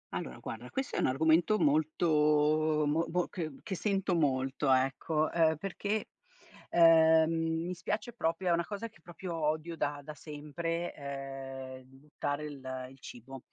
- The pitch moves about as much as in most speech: Yes, average, 3.4 semitones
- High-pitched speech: No, medium, 155 Hz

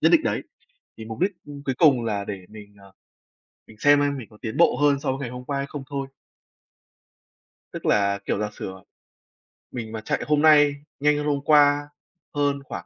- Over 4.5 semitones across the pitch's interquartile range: Yes, average, 5.0 semitones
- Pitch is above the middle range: No, medium, 140 Hz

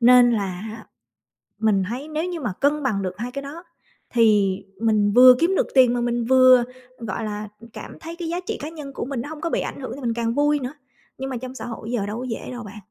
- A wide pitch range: No, average, 4.1 semitones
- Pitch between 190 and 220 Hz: No, high, 245 Hz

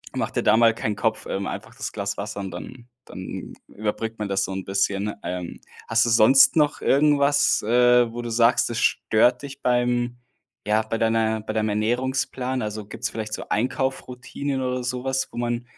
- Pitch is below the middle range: Yes, low, 120 Hz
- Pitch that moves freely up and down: No, average, 2.7 semitones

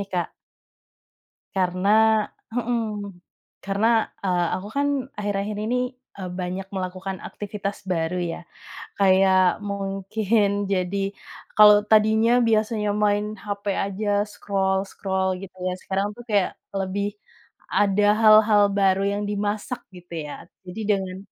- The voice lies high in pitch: Yes, high, 200 Hz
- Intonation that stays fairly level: Yes, narrow, 1.8 semitones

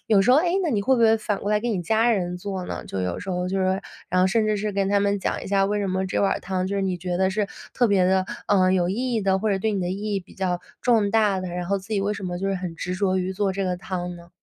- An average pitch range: No, narrow, 2.2 semitones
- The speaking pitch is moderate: No, high, 195 Hz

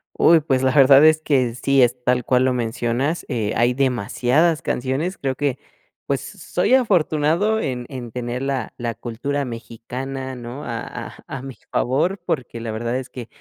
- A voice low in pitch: Yes, low, 130 Hz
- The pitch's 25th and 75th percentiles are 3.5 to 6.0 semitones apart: No, average, 2.9 semitones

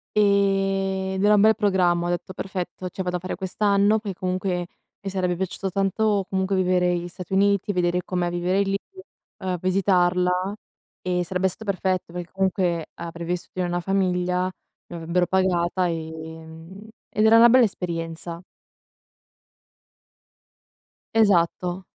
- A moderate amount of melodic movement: No, narrow, 1.8 semitones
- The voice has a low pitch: No, medium, 185 Hz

